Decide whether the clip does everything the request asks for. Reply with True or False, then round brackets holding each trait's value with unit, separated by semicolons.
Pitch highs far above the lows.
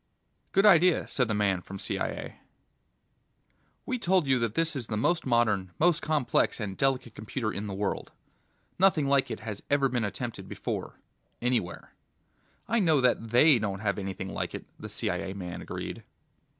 True (6.7 semitones)